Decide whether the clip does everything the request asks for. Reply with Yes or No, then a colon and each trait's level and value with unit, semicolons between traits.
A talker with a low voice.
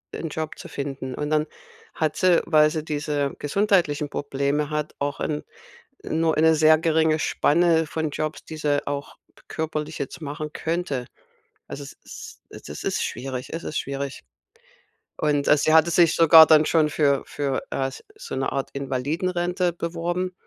No: medium, 155 Hz